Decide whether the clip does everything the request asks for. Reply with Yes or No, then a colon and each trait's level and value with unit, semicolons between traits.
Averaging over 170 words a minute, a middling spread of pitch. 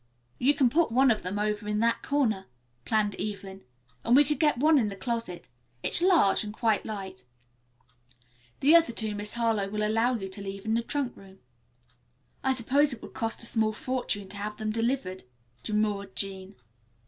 Yes: average, 185 wpm; average, 3.7 semitones